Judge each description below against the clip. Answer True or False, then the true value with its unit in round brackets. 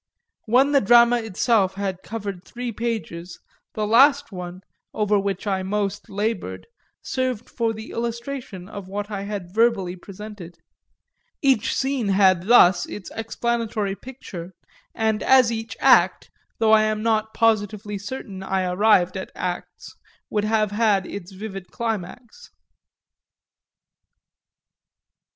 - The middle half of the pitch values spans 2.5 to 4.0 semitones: True (3.1 semitones)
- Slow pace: True (125 wpm)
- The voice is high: True (210 Hz)